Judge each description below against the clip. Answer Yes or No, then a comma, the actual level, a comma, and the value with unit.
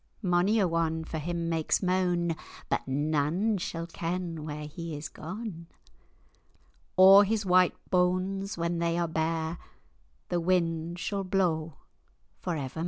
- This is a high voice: No, medium, 170 Hz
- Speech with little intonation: Yes, narrow, 2.3 semitones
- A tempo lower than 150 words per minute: Yes, slow, 135 wpm